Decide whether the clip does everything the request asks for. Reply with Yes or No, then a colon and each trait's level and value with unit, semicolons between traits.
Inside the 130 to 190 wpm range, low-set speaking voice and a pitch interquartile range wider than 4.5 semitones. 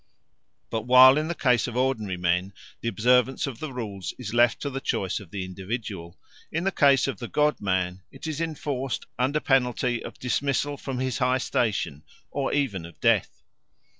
Yes: average, 185 wpm; low, 125 Hz; average, 5.1 semitones